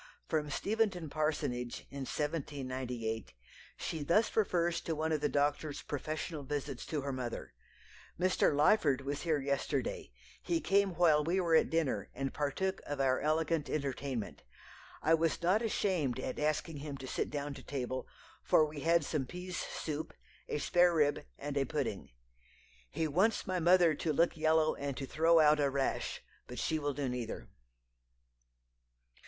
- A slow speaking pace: No, average, 160 wpm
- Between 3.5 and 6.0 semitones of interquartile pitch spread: No, average, 3.1 semitones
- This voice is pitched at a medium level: Yes, medium, 150 Hz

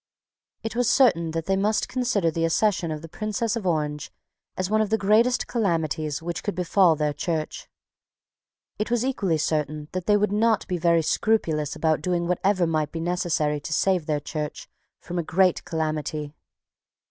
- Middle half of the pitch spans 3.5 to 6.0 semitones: Yes, average, 4.8 semitones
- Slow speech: No, average, 175 wpm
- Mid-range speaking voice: Yes, medium, 170 Hz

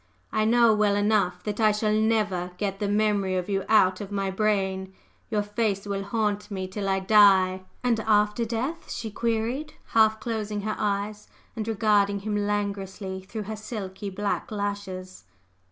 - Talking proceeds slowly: No, average, 165 wpm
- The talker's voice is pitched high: Yes, high, 205 Hz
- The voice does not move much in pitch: Yes, narrow, 1.8 semitones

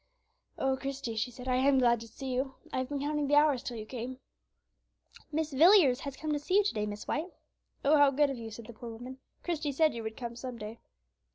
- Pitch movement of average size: Yes, average, 3.6 semitones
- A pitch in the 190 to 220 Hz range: No, very high, 265 Hz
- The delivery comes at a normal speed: No, fast, 245 wpm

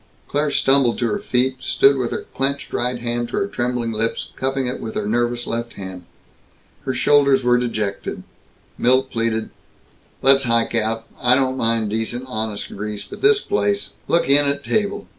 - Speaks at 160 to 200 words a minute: Yes, average, 175 wpm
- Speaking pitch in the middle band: No, low, 120 Hz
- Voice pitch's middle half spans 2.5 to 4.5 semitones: Yes, average, 3.0 semitones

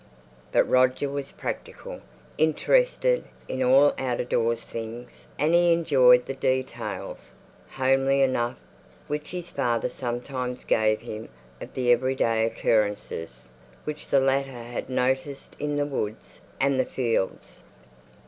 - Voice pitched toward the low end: Yes, low, 130 Hz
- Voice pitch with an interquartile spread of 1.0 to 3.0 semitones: Yes, average, 2.7 semitones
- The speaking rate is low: Yes, slow, 130 wpm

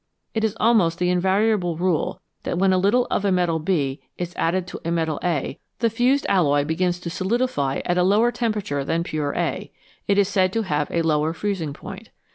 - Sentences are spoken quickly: Yes, fast, 210 wpm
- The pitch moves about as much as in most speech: Yes, average, 4.0 semitones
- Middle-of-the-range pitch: Yes, medium, 180 Hz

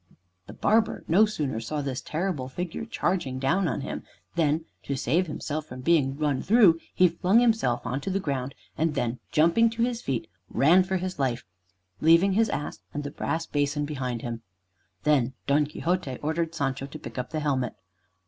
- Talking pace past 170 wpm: Yes, average, 185 wpm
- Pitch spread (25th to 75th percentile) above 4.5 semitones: Yes, average, 5.1 semitones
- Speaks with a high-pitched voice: No, medium, 150 Hz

